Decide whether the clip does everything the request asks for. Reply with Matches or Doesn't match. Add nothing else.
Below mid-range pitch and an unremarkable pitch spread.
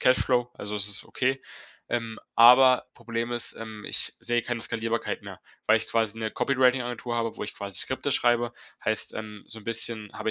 Doesn't match